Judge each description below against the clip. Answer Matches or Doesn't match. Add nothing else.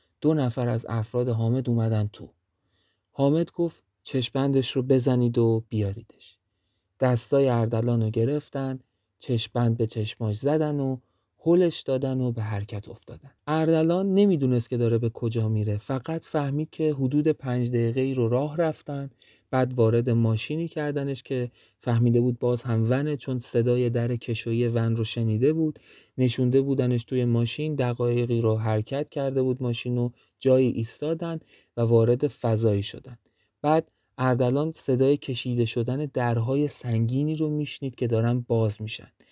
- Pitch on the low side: Matches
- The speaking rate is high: Doesn't match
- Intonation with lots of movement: Doesn't match